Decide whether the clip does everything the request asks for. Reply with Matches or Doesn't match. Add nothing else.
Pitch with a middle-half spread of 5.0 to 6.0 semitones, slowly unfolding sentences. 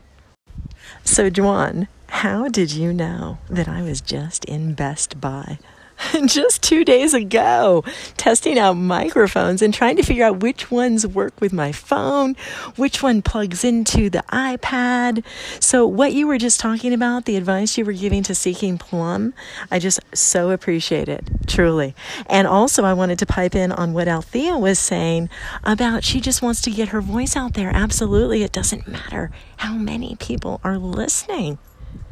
Doesn't match